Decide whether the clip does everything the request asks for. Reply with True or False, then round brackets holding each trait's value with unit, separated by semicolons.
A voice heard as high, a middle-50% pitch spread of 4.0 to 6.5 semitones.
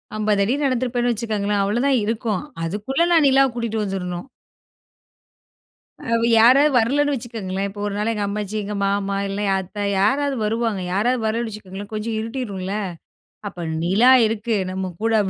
False (215 Hz; 3.2 semitones)